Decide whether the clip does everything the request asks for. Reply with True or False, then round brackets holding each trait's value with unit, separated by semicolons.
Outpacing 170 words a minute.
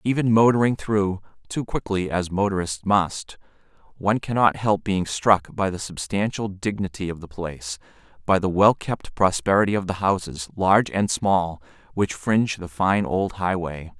False (160 wpm)